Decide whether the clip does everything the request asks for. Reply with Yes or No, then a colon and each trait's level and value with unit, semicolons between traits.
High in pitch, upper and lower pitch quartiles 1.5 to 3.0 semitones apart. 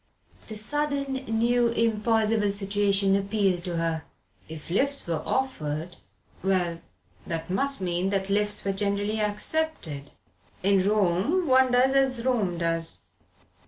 No: high, 205 Hz; average, 5.0 semitones